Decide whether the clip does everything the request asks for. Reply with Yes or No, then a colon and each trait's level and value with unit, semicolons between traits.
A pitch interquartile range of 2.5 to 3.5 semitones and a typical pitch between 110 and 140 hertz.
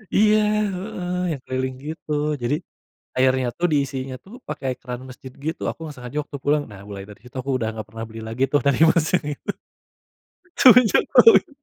No: average, 4.5 semitones; low, 135 Hz